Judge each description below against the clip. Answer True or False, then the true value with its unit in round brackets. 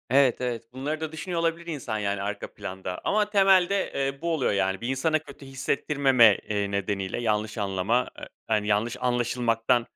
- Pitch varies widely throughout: True (6.1 semitones)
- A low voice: True (125 Hz)